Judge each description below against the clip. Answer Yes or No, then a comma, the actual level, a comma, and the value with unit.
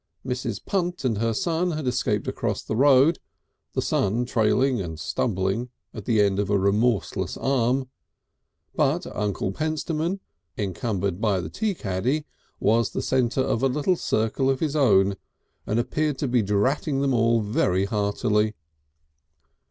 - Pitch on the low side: Yes, low, 115 Hz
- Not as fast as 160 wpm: Yes, average, 150 wpm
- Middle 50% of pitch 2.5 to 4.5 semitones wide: No, average, 5.0 semitones